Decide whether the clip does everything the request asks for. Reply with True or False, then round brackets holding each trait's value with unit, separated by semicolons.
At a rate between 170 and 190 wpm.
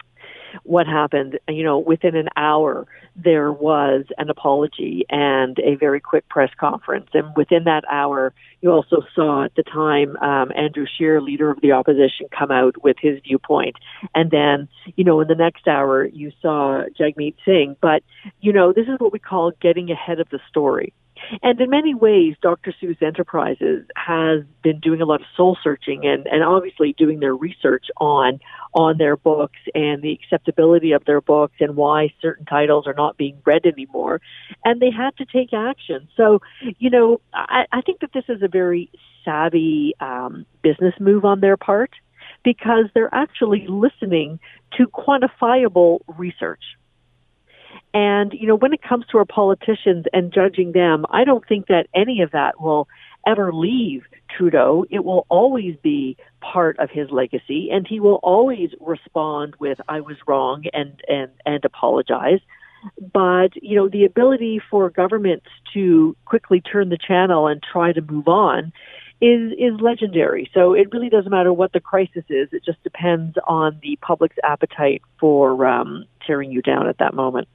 True (175 wpm)